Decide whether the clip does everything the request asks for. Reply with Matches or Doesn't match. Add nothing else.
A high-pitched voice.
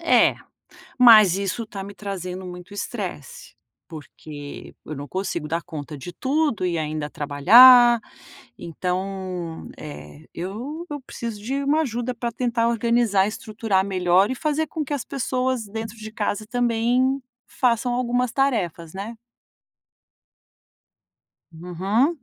Matches